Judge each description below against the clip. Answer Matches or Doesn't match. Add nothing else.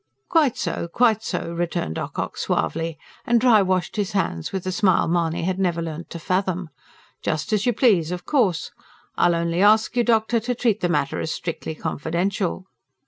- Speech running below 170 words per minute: Doesn't match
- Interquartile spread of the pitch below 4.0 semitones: Doesn't match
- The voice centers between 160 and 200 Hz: Matches